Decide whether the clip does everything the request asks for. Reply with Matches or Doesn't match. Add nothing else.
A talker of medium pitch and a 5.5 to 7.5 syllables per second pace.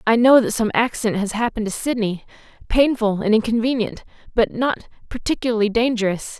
Doesn't match